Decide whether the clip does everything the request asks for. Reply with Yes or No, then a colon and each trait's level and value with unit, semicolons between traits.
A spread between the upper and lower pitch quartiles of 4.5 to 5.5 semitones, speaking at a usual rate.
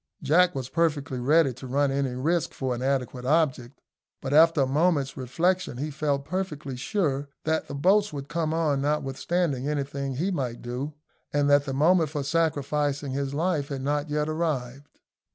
No: average, 2.9 semitones; average, 170 wpm